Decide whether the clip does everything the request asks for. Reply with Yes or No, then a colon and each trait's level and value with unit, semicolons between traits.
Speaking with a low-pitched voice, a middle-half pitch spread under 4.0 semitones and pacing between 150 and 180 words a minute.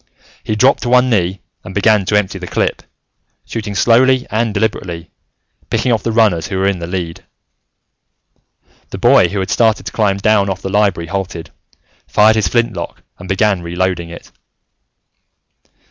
Yes: low, 100 Hz; average, 3.3 semitones; average, 160 wpm